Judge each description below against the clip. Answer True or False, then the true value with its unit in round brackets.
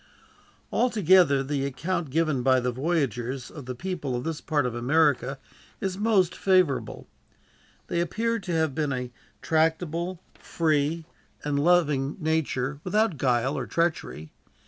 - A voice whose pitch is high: False (155 Hz)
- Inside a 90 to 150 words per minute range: True (140 wpm)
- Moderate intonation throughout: True (4.5 semitones)